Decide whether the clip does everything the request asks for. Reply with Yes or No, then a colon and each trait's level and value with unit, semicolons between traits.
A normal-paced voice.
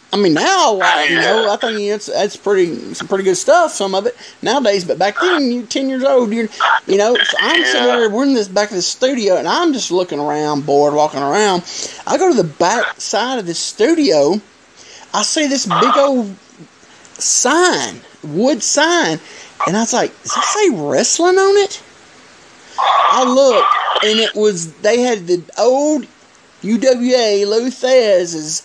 Yes: average, 180 wpm